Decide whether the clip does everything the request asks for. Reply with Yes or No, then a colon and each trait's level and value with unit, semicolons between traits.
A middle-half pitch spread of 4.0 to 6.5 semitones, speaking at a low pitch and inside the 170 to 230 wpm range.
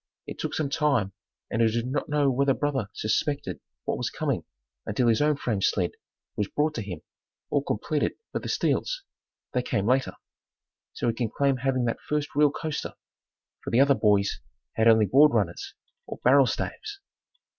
Yes: average, 4.6 semitones; low, 130 Hz; average, 180 wpm